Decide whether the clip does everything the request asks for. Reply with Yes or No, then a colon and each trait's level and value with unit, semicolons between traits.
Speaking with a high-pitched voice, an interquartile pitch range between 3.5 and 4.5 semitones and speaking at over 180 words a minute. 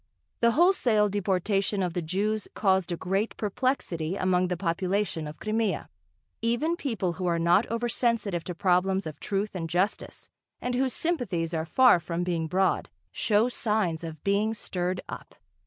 No: high, 195 Hz; average, 3.9 semitones; average, 160 wpm